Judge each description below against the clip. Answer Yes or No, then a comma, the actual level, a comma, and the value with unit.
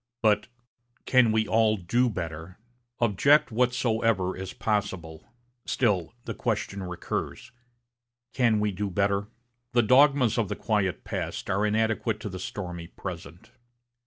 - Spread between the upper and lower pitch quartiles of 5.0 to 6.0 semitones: No, average, 3.5 semitones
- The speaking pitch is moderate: No, low, 105 Hz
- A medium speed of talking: No, slow, 130 wpm